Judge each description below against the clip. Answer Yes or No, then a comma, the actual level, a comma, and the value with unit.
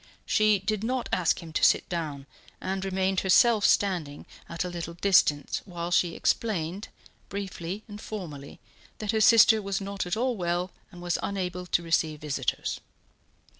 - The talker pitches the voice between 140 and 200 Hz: Yes, medium, 185 Hz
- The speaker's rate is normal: Yes, average, 160 wpm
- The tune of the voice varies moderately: Yes, average, 3.2 semitones